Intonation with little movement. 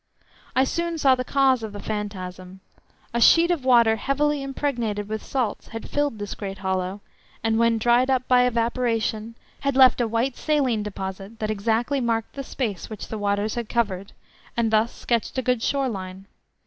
No: average, 3.8 semitones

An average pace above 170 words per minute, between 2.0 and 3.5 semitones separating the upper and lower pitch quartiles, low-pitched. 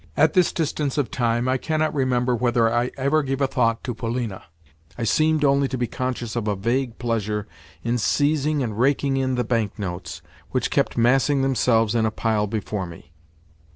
Yes: average, 190 wpm; average, 3.1 semitones; low, 125 Hz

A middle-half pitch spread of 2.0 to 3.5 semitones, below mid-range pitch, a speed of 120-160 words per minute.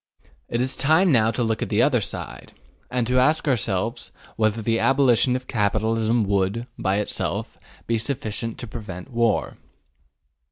Yes: average, 2.8 semitones; low, 115 Hz; average, 155 wpm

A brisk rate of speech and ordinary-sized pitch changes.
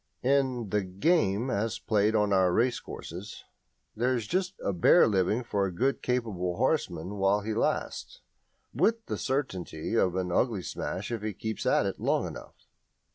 No: average, 165 wpm; average, 4.8 semitones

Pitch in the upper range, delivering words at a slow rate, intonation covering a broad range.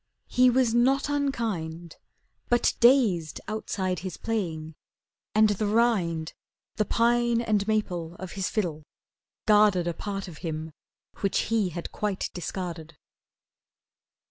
No: high, 200 Hz; slow, 120 wpm; average, 5.0 semitones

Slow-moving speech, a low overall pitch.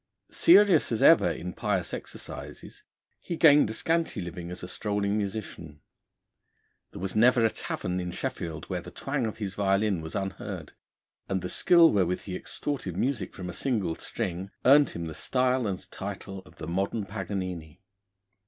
No: average, 160 wpm; low, 100 Hz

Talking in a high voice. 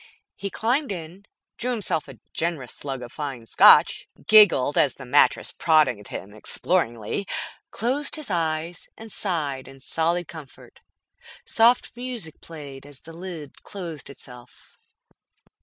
No: medium, 160 Hz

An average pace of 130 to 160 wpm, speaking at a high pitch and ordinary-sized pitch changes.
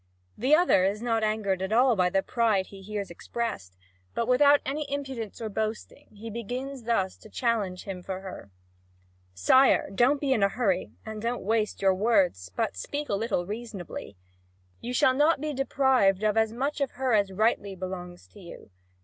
No: average, 180 wpm; high, 220 Hz; average, 4.6 semitones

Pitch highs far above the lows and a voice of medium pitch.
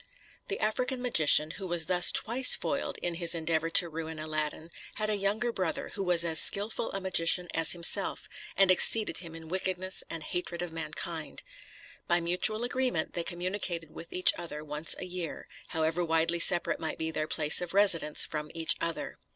No: average, 2.7 semitones; medium, 170 Hz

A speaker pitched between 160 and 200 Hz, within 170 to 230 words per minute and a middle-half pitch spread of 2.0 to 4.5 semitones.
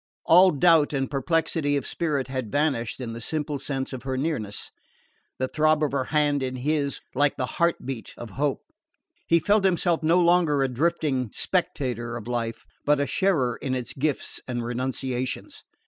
No: medium, 140 Hz; average, 180 wpm; average, 3.6 semitones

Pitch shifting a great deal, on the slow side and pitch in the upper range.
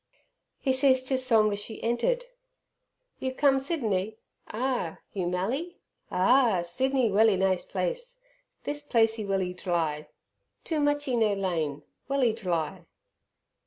Yes: wide, 6.1 semitones; slow, 125 wpm; high, 225 Hz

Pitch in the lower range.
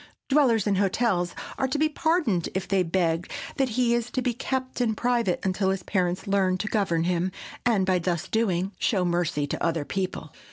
No: high, 190 Hz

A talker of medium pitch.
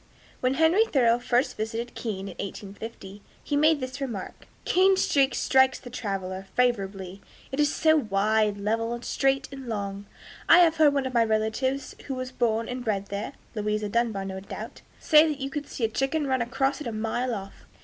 No: high, 240 Hz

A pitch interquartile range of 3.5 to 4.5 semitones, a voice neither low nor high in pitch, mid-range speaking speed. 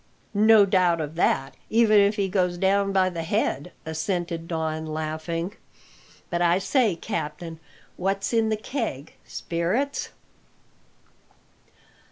No: average, 3.8 semitones; medium, 180 Hz; slow, 120 wpm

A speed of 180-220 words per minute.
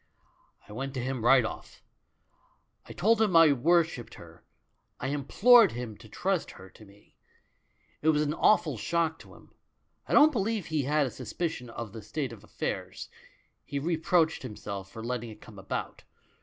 Yes: average, 185 wpm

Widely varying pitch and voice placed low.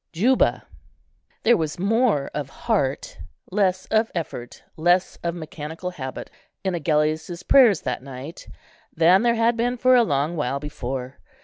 No: wide, 6.7 semitones; medium, 170 Hz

